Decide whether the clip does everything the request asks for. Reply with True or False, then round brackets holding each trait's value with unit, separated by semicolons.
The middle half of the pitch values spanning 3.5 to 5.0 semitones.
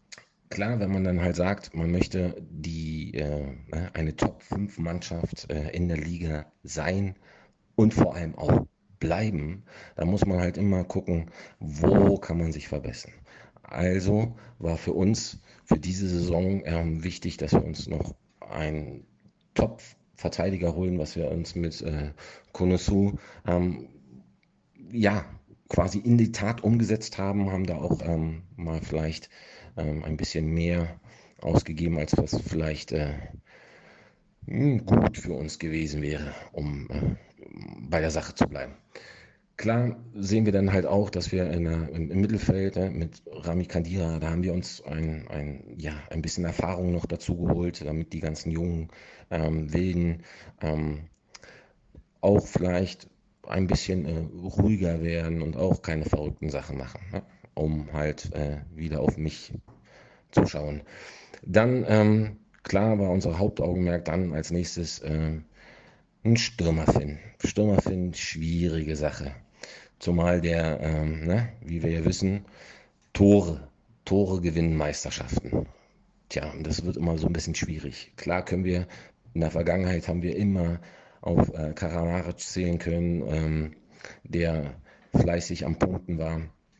False (2.9 semitones)